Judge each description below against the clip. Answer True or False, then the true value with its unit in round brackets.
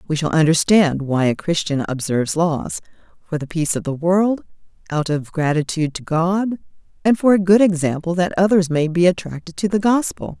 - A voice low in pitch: False (170 Hz)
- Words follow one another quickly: False (185 wpm)